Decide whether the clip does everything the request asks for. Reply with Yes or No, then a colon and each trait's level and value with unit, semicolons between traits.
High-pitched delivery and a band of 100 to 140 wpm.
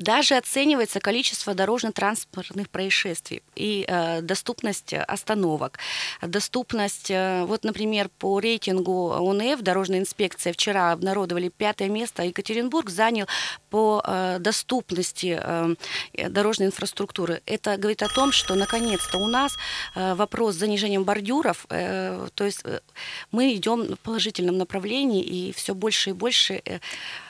Yes: high, 200 Hz; average, 130 wpm